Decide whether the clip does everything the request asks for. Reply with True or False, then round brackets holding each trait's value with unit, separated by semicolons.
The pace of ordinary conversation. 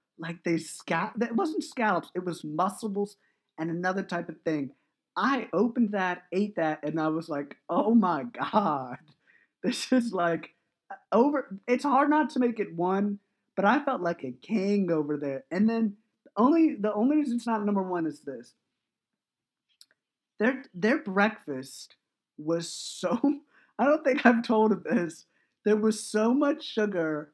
True (160 wpm)